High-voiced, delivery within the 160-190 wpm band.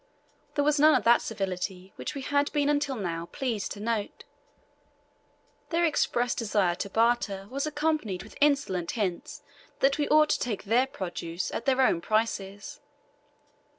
No: high, 230 Hz; average, 150 wpm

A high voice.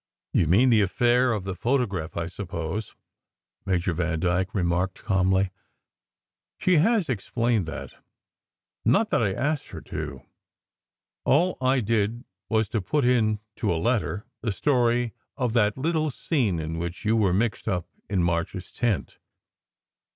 No: low, 105 Hz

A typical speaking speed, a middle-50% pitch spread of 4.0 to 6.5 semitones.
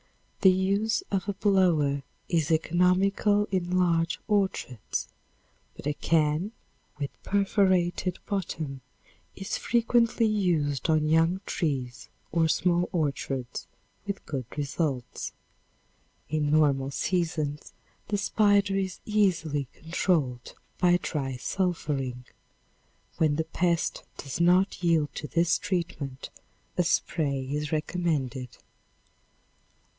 No: slow, 105 wpm; average, 4.5 semitones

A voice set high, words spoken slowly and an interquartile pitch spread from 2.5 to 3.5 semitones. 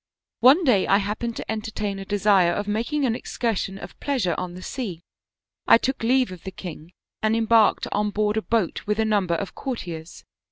No: high, 210 Hz; average, 195 wpm; average, 3.2 semitones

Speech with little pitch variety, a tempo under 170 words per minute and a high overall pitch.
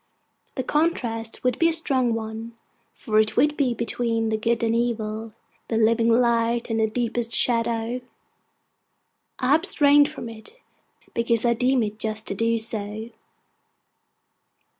Yes: narrow, 1.9 semitones; average, 140 wpm; high, 230 Hz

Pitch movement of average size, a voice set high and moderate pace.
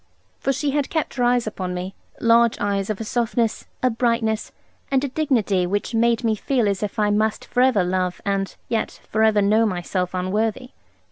Yes: average, 3.4 semitones; high, 220 Hz; average, 195 wpm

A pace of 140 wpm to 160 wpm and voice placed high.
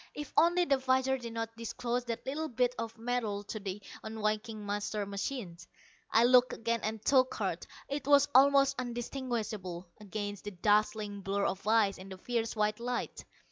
No: average, 170 wpm; high, 225 Hz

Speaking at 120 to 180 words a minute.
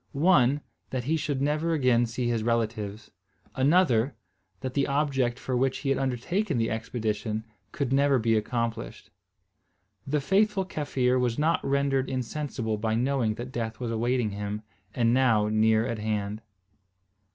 Yes: average, 150 wpm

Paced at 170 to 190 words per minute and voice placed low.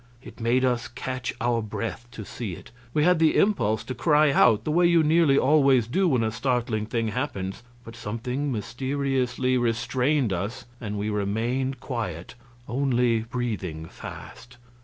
No: average, 160 wpm; low, 120 Hz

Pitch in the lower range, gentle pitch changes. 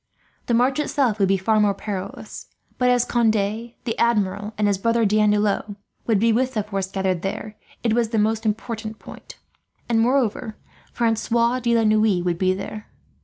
No: high, 220 Hz; narrow, 2.3 semitones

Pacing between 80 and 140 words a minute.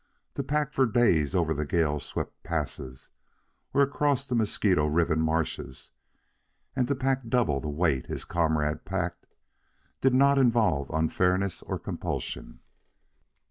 Yes: slow, 135 wpm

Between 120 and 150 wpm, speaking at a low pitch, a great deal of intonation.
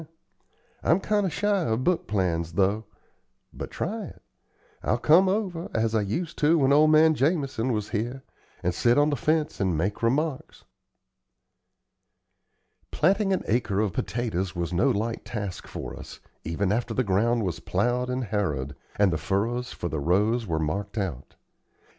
No: average, 165 wpm; low, 115 Hz; wide, 7.5 semitones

